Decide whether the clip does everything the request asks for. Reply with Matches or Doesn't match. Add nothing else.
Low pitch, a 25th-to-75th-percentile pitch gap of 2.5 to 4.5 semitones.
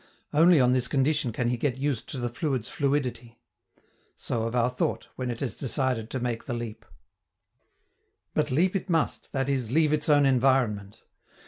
Matches